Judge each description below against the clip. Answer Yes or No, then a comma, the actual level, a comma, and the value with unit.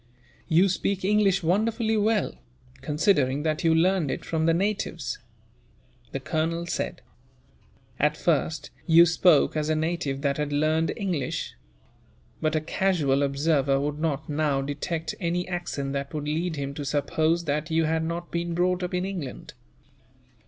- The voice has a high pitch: No, medium, 160 Hz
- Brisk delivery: No, average, 150 wpm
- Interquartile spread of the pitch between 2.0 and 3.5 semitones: Yes, average, 3.2 semitones